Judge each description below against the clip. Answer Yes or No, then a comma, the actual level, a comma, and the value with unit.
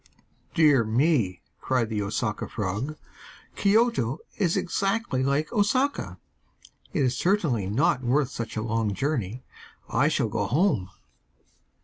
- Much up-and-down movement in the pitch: Yes, wide, 7.3 semitones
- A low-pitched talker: Yes, low, 130 Hz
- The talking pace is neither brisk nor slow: No, slow, 120 wpm